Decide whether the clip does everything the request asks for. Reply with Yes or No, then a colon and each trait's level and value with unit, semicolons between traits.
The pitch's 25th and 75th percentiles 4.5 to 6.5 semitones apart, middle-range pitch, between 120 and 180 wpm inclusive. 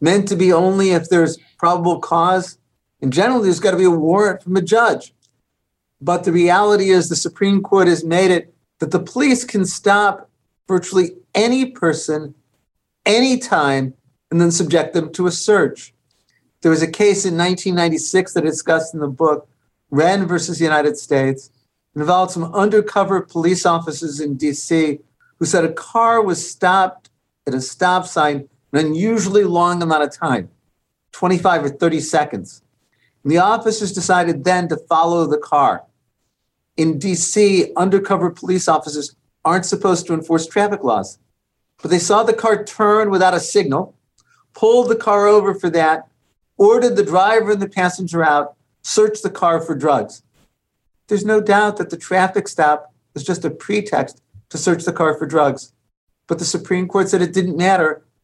No: average, 3.9 semitones; medium, 175 Hz; average, 165 wpm